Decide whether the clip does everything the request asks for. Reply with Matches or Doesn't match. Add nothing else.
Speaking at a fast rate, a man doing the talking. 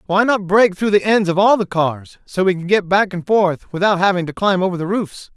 Matches